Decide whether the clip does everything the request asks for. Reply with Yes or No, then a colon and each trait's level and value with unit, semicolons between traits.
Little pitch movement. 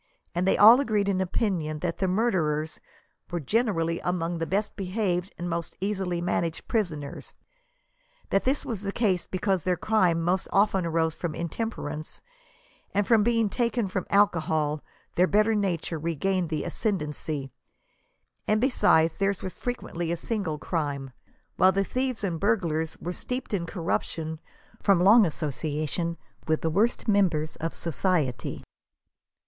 No: average, 4.0 semitones